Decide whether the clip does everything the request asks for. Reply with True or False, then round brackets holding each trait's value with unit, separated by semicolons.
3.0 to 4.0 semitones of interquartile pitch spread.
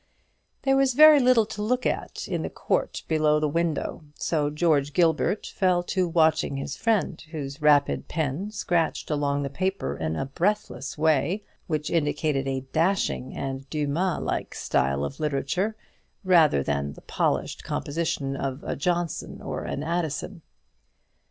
False (4.6 semitones)